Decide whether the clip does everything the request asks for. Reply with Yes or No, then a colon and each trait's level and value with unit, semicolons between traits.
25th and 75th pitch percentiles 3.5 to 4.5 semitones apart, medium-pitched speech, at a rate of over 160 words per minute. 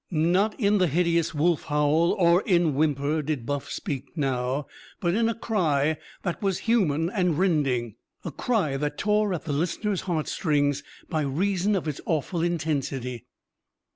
No: average, 4.2 semitones; medium, 160 Hz; average, 155 wpm